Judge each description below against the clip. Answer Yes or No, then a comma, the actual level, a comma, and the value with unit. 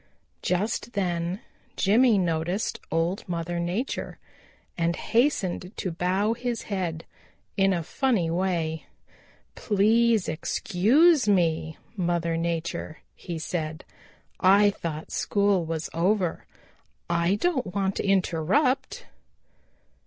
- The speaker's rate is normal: No, slow, 100 wpm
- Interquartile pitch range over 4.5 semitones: No, average, 3.8 semitones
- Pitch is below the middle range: No, medium, 185 Hz